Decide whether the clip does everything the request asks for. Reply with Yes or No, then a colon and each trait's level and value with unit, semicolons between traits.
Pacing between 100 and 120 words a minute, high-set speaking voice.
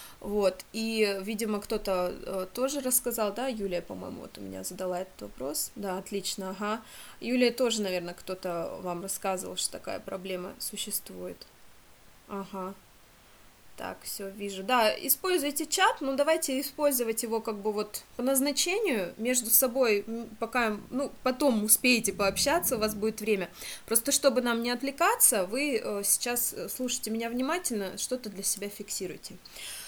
No: average, 140 wpm; high, 220 Hz